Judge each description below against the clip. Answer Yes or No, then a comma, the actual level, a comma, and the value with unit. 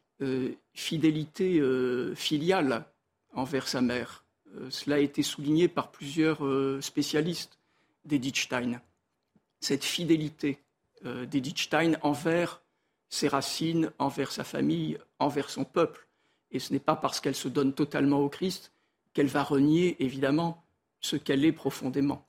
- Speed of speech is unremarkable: No, slow, 130 wpm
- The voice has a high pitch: No, medium, 145 Hz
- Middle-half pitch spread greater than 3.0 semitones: No, narrow, 2.5 semitones